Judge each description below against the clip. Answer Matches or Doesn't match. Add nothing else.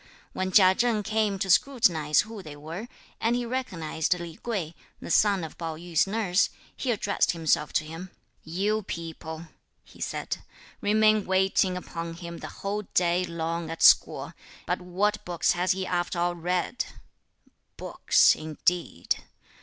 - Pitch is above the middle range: Doesn't match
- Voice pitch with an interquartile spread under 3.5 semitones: Doesn't match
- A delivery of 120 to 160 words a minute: Matches